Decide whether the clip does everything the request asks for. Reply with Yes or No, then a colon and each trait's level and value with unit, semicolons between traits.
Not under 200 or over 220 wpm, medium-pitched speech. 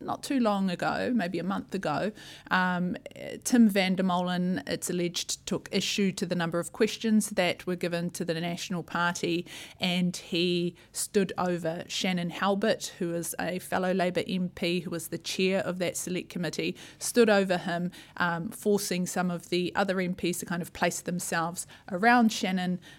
No: average, 170 wpm; medium, 180 Hz